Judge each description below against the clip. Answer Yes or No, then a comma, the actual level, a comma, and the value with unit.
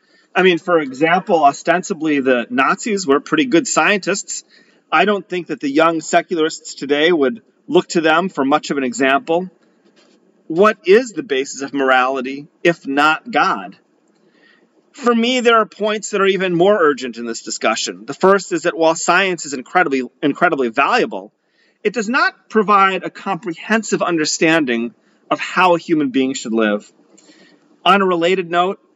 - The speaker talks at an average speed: Yes, average, 160 wpm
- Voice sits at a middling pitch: Yes, medium, 170 Hz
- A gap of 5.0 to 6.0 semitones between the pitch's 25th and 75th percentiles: Yes, wide, 5.4 semitones